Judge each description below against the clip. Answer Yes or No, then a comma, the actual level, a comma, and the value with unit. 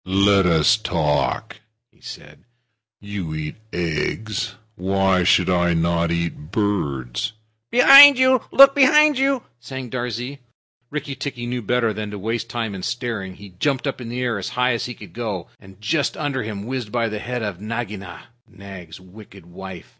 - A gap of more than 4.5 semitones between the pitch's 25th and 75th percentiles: Yes, average, 5.1 semitones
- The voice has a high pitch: No, low, 105 Hz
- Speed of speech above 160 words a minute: Yes, average, 170 wpm